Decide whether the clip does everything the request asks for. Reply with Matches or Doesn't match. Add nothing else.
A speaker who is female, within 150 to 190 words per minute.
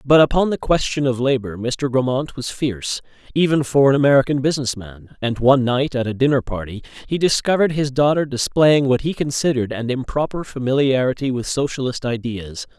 Doesn't match